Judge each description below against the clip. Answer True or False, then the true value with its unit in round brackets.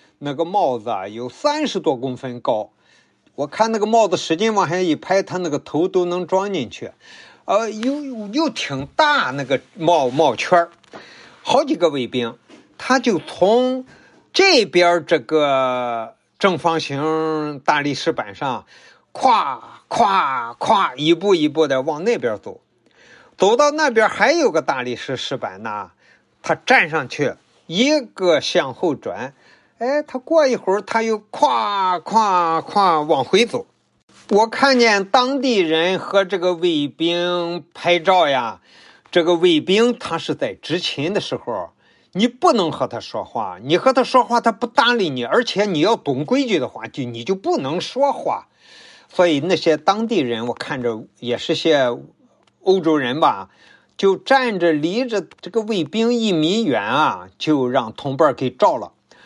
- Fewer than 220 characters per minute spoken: True (210 characters per minute)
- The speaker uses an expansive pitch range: True (6.6 semitones)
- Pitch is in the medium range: True (180 Hz)